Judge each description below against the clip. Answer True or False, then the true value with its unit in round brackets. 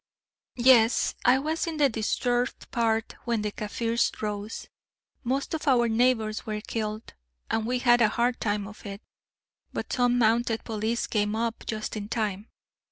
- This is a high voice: True (230 Hz)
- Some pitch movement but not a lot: False (2.3 semitones)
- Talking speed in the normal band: True (160 wpm)